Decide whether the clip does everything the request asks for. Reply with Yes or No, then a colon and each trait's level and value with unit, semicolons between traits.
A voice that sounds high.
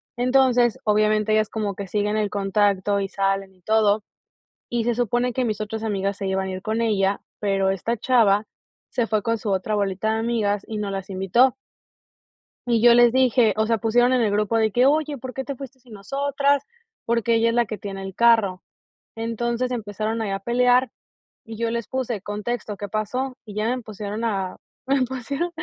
Yes: high, 220 Hz